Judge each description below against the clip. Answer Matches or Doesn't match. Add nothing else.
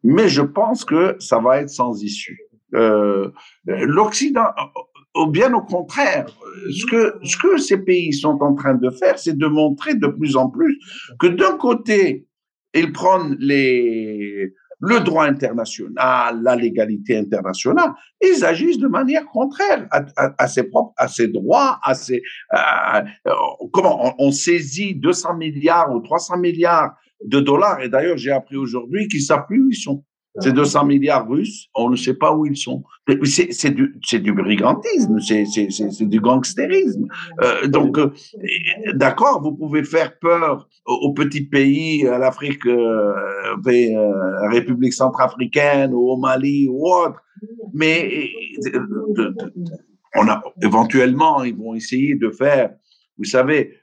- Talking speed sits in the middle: Matches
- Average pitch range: Doesn't match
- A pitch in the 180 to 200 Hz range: Doesn't match